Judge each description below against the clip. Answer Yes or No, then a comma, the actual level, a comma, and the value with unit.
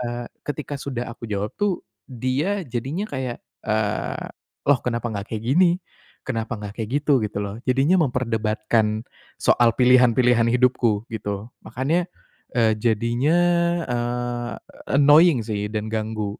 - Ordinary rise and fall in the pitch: Yes, average, 3.3 semitones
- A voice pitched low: Yes, low, 120 Hz